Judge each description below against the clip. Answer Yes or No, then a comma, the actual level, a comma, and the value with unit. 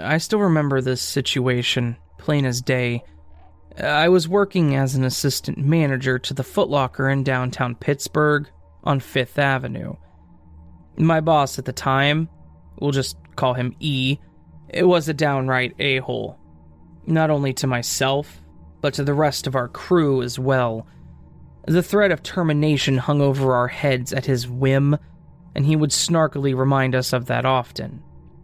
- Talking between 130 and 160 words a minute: Yes, average, 155 wpm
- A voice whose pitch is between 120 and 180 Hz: Yes, low, 135 Hz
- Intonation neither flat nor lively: Yes, average, 3.1 semitones